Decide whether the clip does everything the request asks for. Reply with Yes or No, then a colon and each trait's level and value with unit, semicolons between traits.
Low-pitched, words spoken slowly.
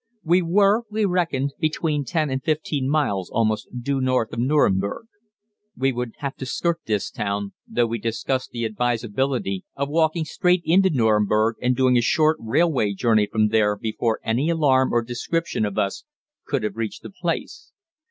No: low, 130 Hz; average, 170 wpm